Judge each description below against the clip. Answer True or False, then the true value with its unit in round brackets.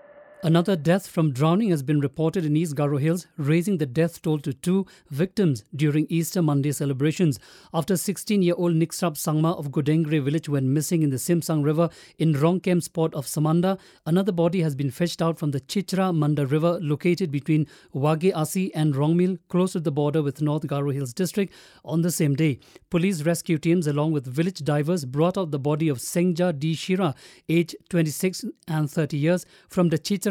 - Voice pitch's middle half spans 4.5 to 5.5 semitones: False (3.0 semitones)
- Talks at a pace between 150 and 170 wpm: False (180 wpm)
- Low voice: False (165 Hz)